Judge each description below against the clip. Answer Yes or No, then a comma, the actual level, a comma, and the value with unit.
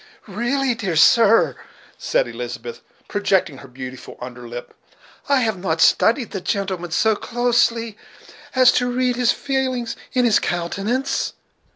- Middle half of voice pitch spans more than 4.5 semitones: Yes, wide, 5.5 semitones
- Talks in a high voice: Yes, high, 225 Hz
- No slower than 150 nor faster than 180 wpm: No, slow, 135 wpm